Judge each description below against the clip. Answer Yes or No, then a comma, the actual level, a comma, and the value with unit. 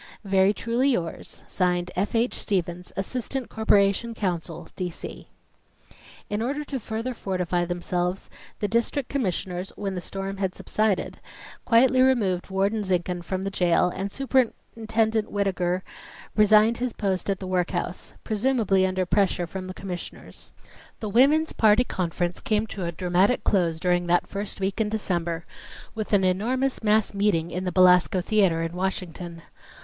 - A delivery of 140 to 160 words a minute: Yes, average, 150 wpm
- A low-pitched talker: No, high, 195 Hz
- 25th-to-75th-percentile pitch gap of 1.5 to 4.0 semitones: Yes, average, 3.5 semitones